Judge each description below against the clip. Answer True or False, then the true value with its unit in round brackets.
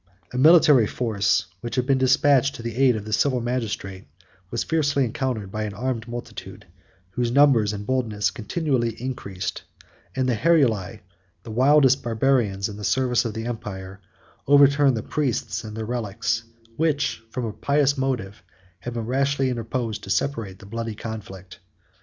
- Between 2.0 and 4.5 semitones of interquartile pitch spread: True (3.7 semitones)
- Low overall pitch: True (120 Hz)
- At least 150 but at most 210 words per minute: True (160 wpm)